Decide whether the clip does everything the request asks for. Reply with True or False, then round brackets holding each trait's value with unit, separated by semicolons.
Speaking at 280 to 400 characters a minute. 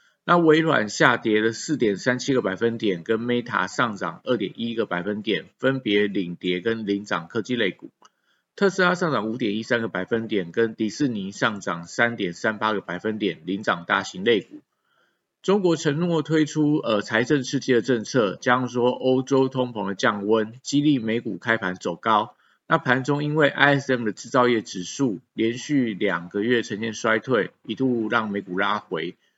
False (270 characters per minute)